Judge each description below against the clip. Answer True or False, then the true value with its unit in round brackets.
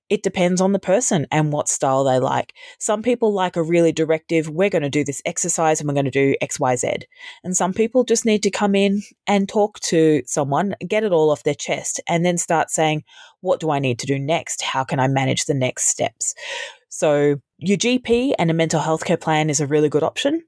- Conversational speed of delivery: False (230 wpm)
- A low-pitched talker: False (170 Hz)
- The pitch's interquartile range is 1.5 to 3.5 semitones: False (5.4 semitones)